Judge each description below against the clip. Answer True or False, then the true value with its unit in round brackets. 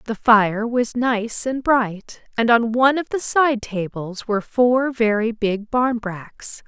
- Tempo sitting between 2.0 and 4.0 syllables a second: True (3.7 syllables/s)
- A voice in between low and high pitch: False (230 Hz)